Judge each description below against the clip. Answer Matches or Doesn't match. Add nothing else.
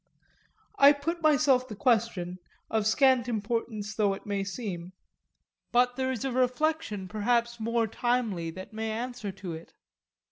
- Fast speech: Doesn't match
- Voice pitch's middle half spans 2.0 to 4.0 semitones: Matches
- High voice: Matches